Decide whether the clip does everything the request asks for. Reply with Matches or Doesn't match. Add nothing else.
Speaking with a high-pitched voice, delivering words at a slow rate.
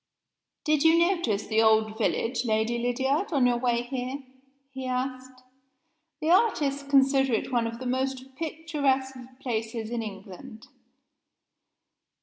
Matches